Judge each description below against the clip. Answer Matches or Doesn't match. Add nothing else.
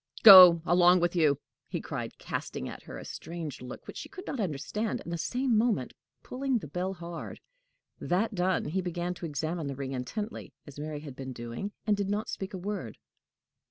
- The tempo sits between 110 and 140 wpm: Doesn't match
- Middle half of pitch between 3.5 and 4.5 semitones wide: Doesn't match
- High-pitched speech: Doesn't match